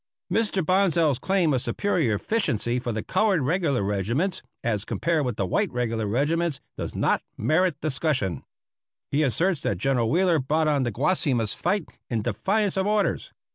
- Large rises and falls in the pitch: Yes, wide, 7.4 semitones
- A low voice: No, medium, 150 Hz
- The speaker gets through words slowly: No, average, 160 wpm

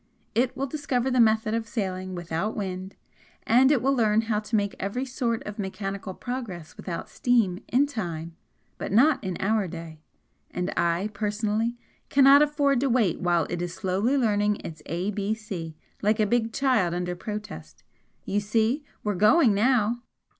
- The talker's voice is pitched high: Yes, high, 210 Hz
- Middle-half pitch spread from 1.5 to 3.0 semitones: No, average, 4.6 semitones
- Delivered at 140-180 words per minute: Yes, average, 160 wpm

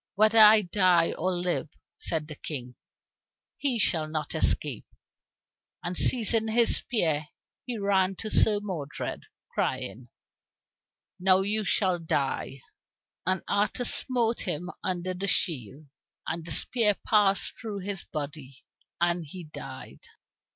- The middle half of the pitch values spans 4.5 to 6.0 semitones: Yes, average, 5.0 semitones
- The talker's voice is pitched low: No, medium, 185 Hz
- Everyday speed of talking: No, slow, 125 wpm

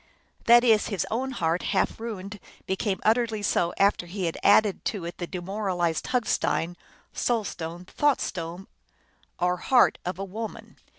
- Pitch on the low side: No, high, 195 Hz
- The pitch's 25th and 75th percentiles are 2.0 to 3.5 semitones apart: No, average, 3.9 semitones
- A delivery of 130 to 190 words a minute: Yes, average, 160 wpm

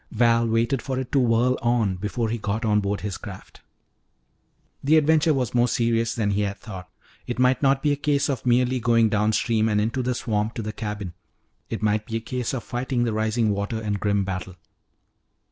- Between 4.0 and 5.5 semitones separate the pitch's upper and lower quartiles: No, average, 3.0 semitones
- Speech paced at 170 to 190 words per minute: No, fast, 205 wpm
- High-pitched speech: No, low, 115 Hz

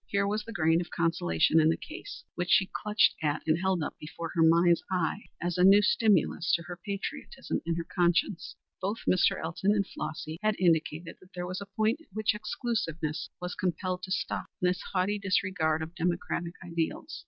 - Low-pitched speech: No, medium, 180 Hz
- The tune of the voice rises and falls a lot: No, average, 3.3 semitones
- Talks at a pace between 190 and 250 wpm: Yes, average, 195 wpm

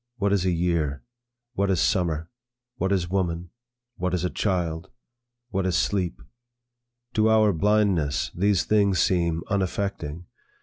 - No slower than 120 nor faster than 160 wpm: Yes, slow, 135 wpm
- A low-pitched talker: Yes, very low, 90 Hz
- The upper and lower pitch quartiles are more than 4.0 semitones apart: No, average, 3.0 semitones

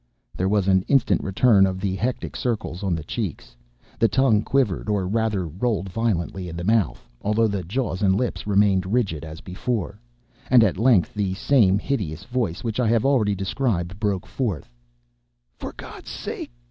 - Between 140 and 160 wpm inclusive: No, average, 170 wpm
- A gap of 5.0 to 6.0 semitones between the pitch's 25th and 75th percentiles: No, average, 3.7 semitones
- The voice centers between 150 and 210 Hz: No, low, 100 Hz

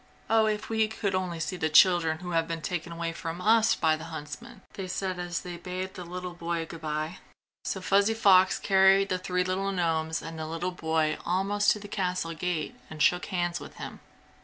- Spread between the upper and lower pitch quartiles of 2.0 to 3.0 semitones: Yes, narrow, 2.6 semitones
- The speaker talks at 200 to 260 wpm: Yes, fast, 205 wpm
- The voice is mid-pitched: Yes, medium, 180 Hz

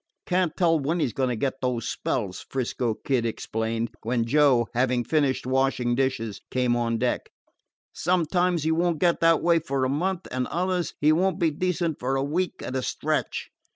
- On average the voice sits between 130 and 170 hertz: Yes, low, 135 Hz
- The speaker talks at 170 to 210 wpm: Yes, average, 190 wpm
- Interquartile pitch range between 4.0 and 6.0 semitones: Yes, average, 5.3 semitones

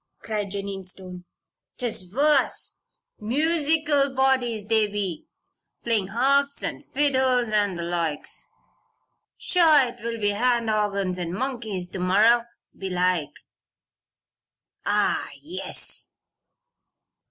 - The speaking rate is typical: No, slow, 95 wpm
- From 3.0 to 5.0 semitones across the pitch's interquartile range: No, wide, 5.6 semitones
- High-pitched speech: Yes, high, 220 Hz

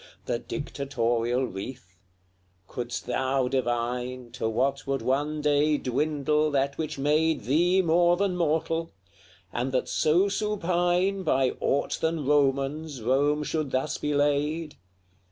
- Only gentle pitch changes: No, average, 3.6 semitones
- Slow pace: Yes, slow, 125 wpm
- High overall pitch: No, medium, 145 Hz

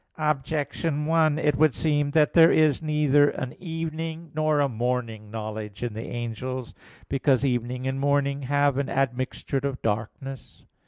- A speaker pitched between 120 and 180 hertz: Yes, medium, 140 Hz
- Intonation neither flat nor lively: Yes, average, 3.4 semitones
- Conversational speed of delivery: Yes, average, 150 wpm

